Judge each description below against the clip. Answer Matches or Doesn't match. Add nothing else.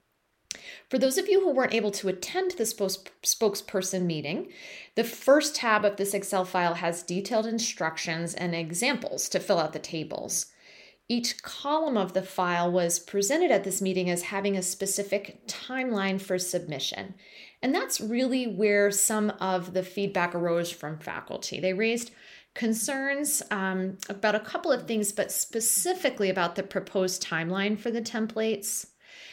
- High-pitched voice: Matches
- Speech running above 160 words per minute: Doesn't match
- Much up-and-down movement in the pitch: Doesn't match